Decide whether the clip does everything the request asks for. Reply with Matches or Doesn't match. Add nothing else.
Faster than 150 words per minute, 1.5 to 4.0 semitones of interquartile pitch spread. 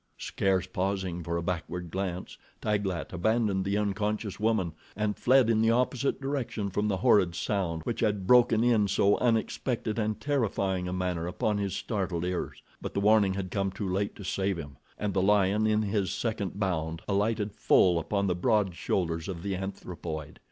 Matches